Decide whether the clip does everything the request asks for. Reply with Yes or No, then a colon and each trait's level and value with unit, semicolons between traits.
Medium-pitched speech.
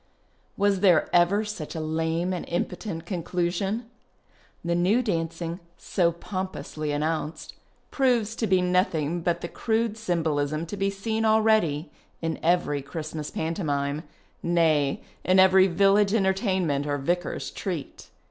Yes: medium, 175 Hz